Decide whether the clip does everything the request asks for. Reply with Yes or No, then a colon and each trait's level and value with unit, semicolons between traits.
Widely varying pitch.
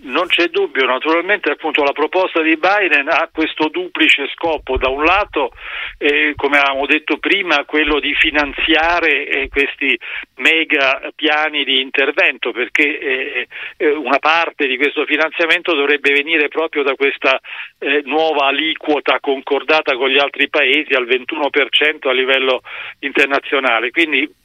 No: average, 2.7 semitones